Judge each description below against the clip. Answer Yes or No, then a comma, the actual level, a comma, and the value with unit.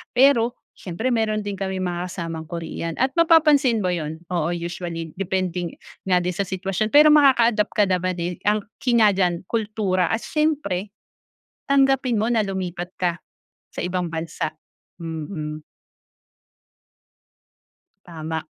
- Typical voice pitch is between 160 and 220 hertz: Yes, medium, 185 Hz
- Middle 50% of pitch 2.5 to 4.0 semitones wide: No, average, 4.6 semitones